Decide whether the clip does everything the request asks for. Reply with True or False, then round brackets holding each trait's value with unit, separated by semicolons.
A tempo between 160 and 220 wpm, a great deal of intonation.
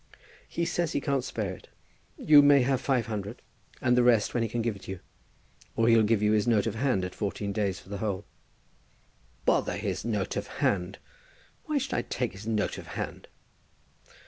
False (195 wpm; 3.6 semitones)